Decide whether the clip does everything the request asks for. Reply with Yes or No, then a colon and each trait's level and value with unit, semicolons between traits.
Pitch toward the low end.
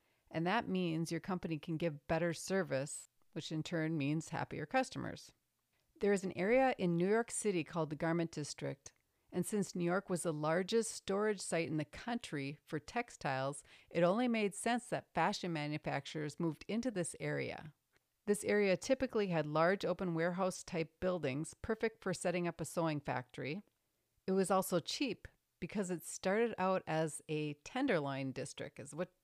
No: medium, 170 Hz